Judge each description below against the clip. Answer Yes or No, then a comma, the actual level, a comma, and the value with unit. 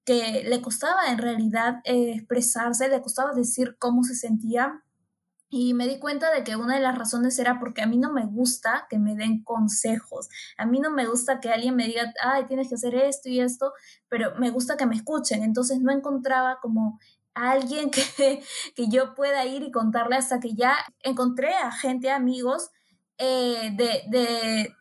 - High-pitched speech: Yes, very high, 250 Hz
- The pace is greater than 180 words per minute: Yes, fast, 190 wpm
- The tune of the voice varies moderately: No, narrow, 2.2 semitones